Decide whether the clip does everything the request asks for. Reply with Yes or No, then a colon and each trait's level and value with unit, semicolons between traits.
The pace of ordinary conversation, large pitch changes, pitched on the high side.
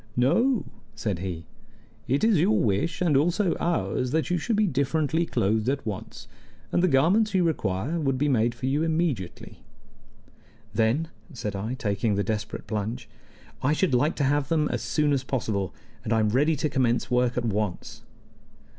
No: average, 175 wpm; wide, 6.5 semitones; low, 135 Hz